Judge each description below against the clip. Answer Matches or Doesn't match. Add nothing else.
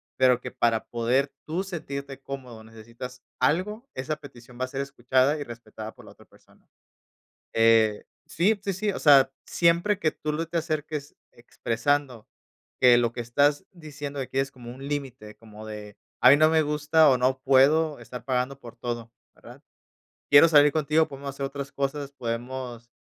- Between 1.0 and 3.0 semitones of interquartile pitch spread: Doesn't match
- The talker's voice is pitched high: Doesn't match